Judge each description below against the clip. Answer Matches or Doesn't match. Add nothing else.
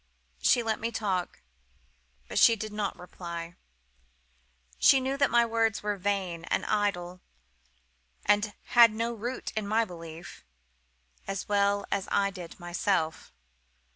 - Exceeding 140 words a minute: Doesn't match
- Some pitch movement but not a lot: Matches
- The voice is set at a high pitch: Matches